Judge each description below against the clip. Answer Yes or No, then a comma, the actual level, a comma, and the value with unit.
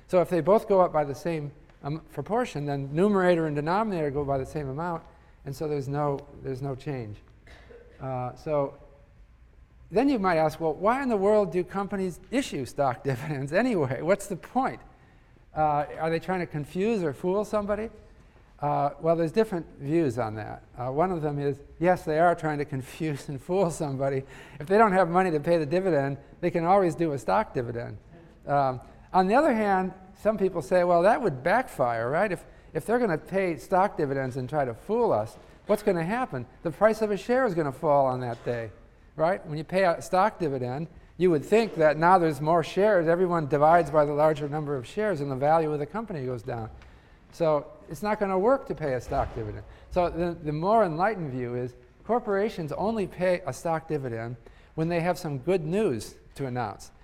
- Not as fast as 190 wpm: No, fast, 205 wpm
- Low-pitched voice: No, medium, 160 Hz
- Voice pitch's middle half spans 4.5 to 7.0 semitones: Yes, average, 5.1 semitones